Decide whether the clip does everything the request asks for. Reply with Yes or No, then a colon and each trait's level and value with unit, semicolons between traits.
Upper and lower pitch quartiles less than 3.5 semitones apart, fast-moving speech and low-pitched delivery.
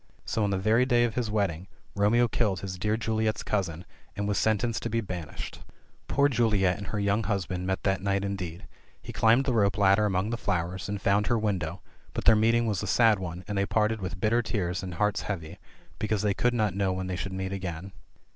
Yes: average, 2.8 semitones; fast, 225 wpm; low, 100 Hz